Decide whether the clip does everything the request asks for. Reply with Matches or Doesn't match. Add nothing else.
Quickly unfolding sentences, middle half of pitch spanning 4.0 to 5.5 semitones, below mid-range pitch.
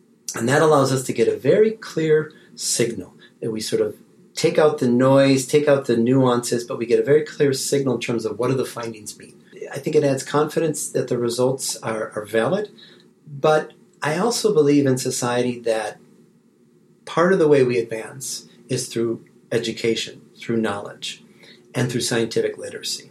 Doesn't match